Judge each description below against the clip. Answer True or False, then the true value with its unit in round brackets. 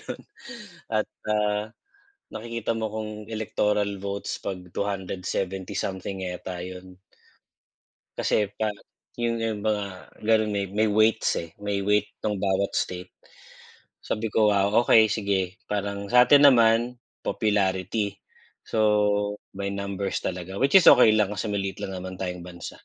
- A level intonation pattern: True (2.1 semitones)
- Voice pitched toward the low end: True (105 Hz)